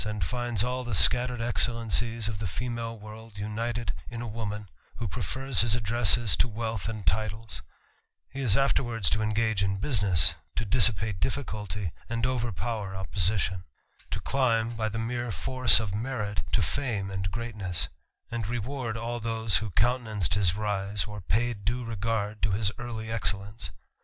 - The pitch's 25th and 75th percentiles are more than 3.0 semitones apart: No, narrow, 2.6 semitones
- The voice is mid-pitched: No, low, 110 Hz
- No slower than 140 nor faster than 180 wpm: Yes, average, 155 wpm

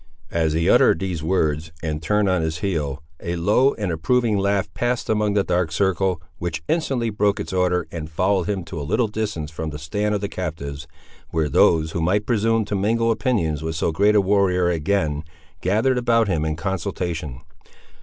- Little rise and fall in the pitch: No, average, 4.5 semitones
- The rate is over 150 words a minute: Yes, average, 190 wpm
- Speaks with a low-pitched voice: Yes, very low, 90 Hz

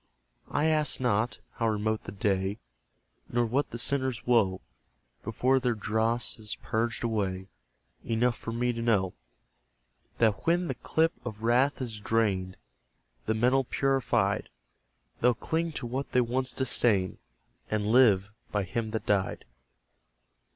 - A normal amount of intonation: Yes, average, 3.1 semitones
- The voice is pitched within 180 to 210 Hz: No, low, 115 Hz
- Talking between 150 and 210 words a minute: No, slow, 135 wpm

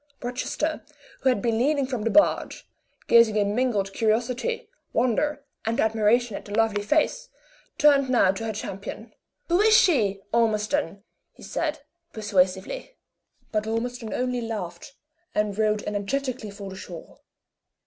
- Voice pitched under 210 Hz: No, high, 225 Hz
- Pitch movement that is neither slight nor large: Yes, average, 3.7 semitones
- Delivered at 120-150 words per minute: Yes, average, 140 wpm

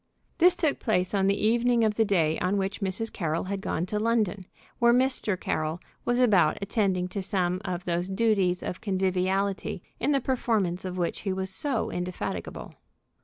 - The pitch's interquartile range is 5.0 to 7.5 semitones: No, average, 3.6 semitones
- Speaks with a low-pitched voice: No, high, 195 Hz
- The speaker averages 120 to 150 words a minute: No, average, 175 wpm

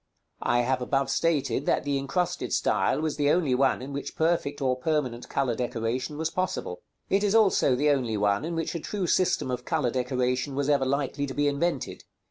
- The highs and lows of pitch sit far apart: No, average, 4.1 semitones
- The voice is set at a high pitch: No, medium, 140 Hz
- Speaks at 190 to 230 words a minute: Yes, average, 200 wpm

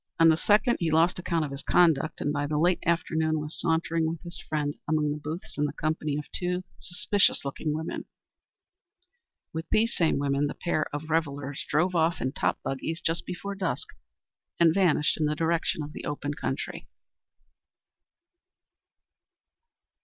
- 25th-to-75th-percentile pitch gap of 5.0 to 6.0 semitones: No, narrow, 2.4 semitones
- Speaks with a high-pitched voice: No, medium, 160 Hz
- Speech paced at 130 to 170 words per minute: Yes, average, 165 wpm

